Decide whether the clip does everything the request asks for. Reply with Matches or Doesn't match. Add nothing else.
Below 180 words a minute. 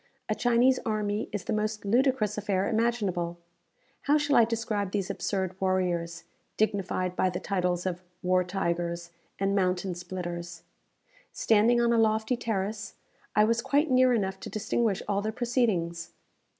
Matches